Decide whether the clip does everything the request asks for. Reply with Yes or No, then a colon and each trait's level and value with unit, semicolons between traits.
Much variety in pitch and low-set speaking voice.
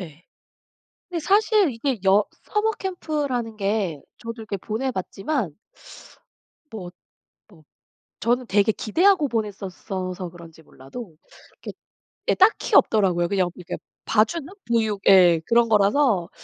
No: wide, 6.0 semitones; high, 215 Hz